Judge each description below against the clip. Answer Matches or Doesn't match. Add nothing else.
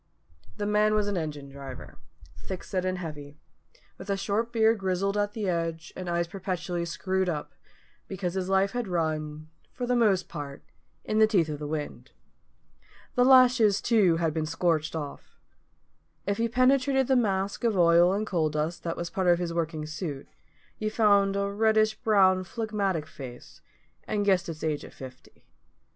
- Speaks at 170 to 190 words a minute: Matches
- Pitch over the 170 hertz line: Matches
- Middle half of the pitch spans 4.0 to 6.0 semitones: Matches